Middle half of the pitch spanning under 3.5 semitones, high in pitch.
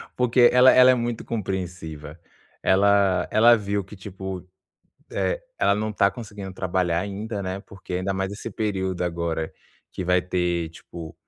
No: average, 2.9 semitones; very low, 95 Hz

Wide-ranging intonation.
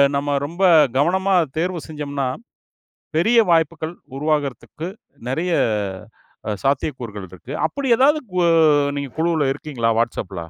No: average, 4.2 semitones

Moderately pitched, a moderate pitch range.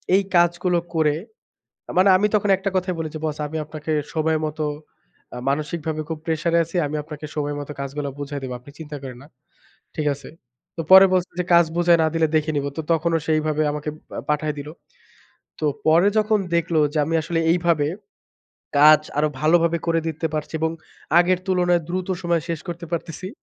No: medium, 160 Hz; narrow, 2.3 semitones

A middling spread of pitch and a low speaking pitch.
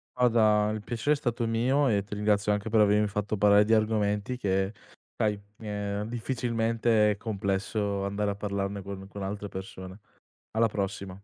No: narrow, 2.0 semitones; low, 105 Hz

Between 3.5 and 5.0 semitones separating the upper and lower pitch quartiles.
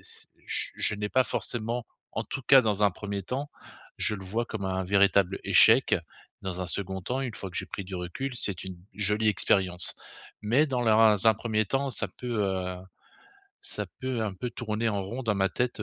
Yes: average, 3.8 semitones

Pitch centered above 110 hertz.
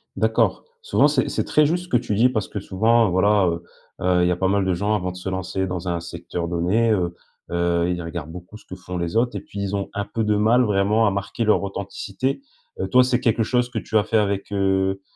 No: low, 100 Hz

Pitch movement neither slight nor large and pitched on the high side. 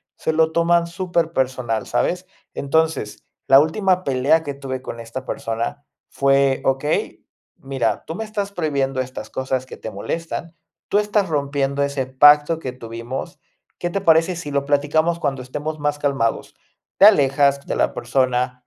No: average, 3.7 semitones; medium, 140 Hz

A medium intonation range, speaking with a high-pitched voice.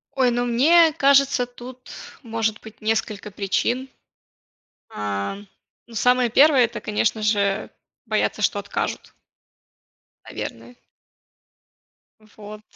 Yes: average, 3.1 semitones; high, 230 Hz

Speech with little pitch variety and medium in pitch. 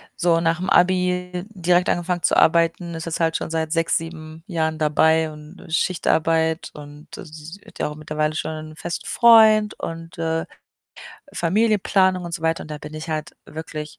Yes: narrow, 2.3 semitones; medium, 165 Hz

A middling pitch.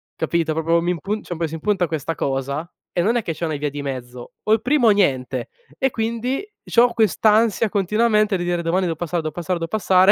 Yes: medium, 175 Hz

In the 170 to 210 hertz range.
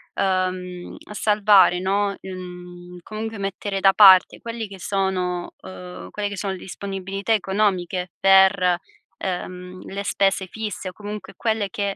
Yes: high, 190 Hz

